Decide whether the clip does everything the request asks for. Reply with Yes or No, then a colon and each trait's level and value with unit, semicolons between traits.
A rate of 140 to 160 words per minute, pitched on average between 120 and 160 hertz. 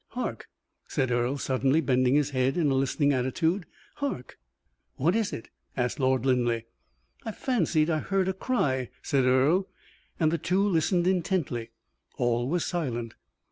Yes: average, 150 wpm; medium, 140 Hz